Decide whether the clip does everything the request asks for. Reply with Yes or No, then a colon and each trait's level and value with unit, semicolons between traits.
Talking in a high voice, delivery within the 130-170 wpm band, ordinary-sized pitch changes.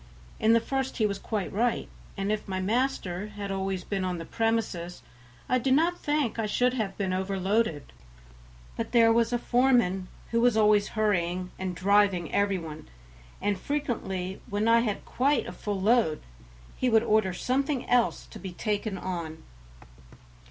Yes: high, 210 Hz; average, 165 wpm; average, 3.9 semitones